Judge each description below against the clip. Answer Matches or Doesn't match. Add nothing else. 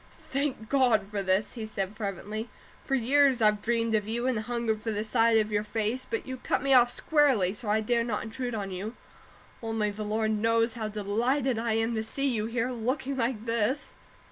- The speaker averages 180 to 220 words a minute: Matches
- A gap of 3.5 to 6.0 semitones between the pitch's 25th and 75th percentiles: Doesn't match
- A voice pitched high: Matches